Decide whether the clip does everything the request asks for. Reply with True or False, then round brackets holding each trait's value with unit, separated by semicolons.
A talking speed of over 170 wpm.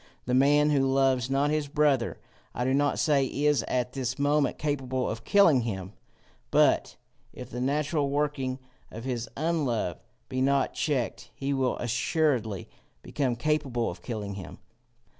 False (150 wpm)